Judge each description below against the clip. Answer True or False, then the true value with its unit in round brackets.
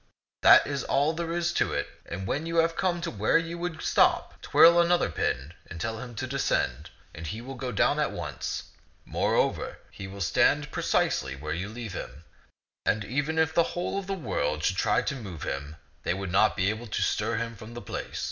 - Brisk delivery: True (210 wpm)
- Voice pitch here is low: True (115 Hz)